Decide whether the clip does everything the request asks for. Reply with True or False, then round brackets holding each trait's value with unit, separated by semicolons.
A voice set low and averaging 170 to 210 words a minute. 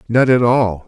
True (115 Hz; 205 wpm)